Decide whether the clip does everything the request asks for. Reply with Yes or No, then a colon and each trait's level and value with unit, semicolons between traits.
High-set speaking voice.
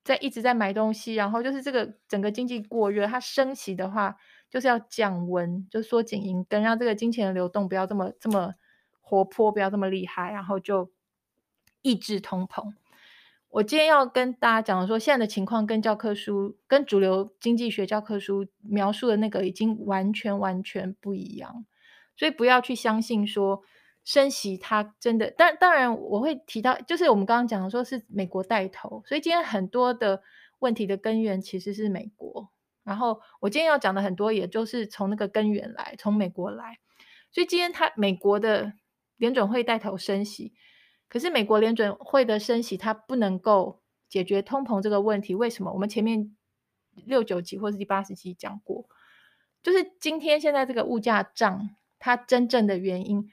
Yes: high, 215 Hz